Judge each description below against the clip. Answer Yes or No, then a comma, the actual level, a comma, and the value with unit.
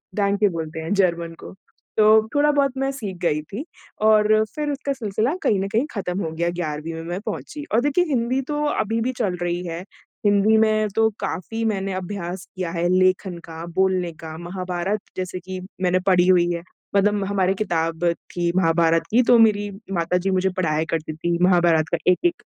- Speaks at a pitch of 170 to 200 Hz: Yes, medium, 185 Hz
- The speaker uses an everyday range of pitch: Yes, average, 3.9 semitones